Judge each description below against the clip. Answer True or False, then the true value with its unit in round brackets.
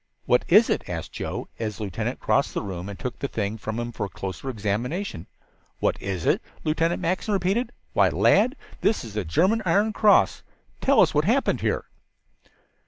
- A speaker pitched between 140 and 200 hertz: False (125 Hz)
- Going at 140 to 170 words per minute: False (185 wpm)